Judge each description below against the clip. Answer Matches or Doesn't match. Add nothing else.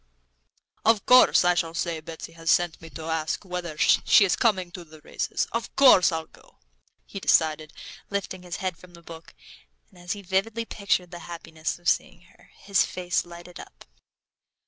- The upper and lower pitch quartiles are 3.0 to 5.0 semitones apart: Doesn't match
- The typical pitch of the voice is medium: Matches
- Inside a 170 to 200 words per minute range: Matches